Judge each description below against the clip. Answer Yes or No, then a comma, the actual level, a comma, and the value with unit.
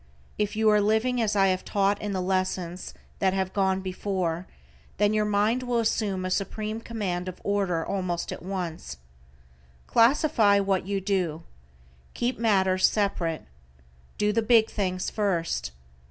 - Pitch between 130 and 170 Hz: No, high, 195 Hz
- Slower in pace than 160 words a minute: Yes, average, 150 wpm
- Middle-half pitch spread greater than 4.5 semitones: No, narrow, 2.4 semitones